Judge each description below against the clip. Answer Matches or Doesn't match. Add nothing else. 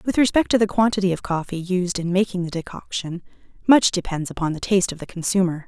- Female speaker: Matches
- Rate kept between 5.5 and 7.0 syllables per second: Matches